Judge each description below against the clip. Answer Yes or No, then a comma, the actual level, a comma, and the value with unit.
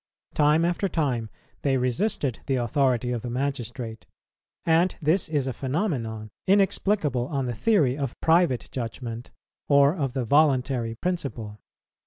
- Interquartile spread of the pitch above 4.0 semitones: Yes, average, 4.7 semitones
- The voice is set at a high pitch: No, low, 135 Hz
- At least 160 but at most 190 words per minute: No, slow, 135 wpm